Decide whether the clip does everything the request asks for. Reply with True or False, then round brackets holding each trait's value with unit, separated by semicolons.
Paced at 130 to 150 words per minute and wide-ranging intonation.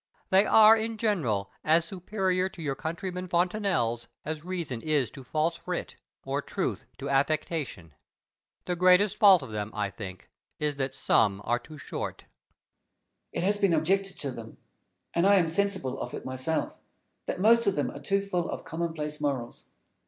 False (170 wpm; 6.0 semitones)